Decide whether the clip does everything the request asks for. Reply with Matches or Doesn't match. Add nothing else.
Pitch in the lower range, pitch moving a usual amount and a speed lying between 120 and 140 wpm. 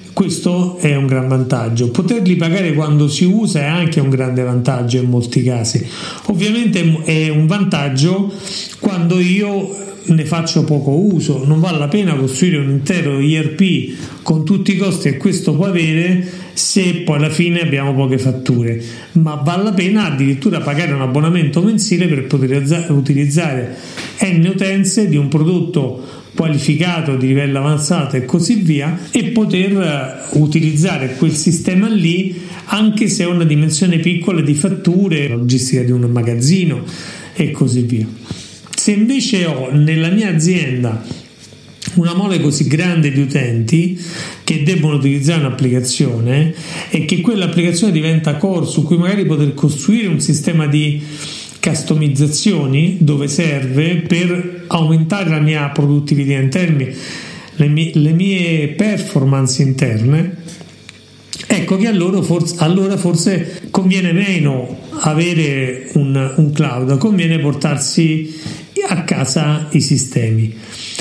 Doesn't match